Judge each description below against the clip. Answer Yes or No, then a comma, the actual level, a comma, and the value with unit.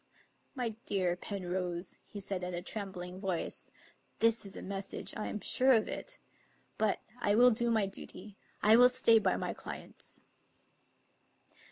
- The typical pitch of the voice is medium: No, high, 205 Hz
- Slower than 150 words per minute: No, average, 165 wpm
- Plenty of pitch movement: No, average, 3.5 semitones